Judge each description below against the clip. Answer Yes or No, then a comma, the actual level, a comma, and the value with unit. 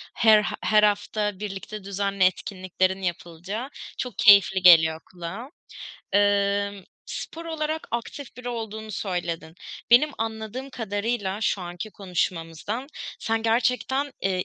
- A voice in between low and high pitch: No, high, 205 Hz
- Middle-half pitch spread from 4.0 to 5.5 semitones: No, average, 3.4 semitones